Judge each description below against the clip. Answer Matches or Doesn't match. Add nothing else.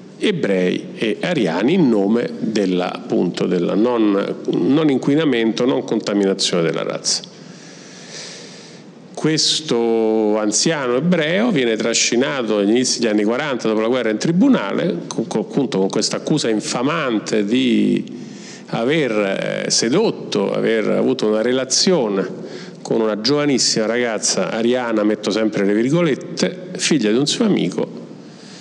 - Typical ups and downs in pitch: Matches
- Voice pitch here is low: Matches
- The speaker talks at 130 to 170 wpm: Doesn't match